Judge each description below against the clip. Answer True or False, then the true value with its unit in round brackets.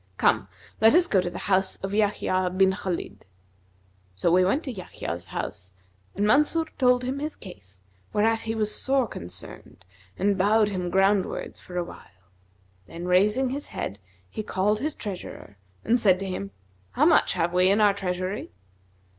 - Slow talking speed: False (170 wpm)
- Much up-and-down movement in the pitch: False (3.5 semitones)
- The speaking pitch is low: False (195 Hz)